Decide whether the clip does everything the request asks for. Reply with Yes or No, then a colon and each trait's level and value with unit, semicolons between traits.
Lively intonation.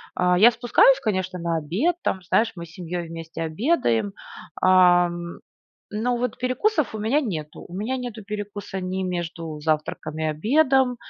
Yes: wide, 6.1 semitones